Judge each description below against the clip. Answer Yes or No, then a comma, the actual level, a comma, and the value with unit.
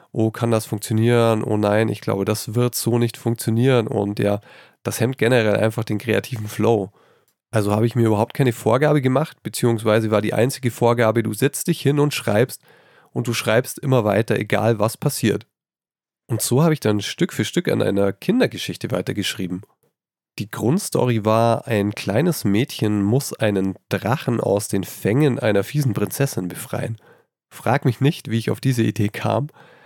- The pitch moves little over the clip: No, average, 3.1 semitones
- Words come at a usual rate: Yes, average, 175 wpm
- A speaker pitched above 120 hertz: No, low, 115 Hz